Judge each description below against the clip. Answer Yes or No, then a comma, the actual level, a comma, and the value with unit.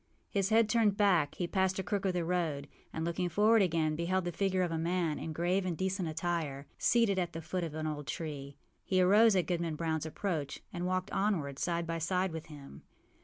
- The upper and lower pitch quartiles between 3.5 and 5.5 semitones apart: No, average, 3.0 semitones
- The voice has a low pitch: No, medium, 175 Hz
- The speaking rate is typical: No, fast, 225 wpm